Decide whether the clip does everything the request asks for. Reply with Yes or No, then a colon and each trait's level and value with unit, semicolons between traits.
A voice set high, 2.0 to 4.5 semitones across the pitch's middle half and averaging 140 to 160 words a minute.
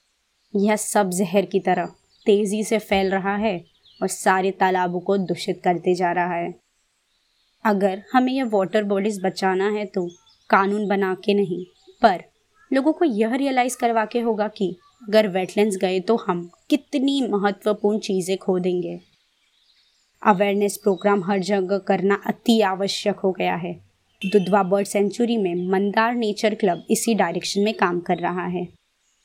Yes: high, 200 Hz; narrow, 2.4 semitones; average, 150 wpm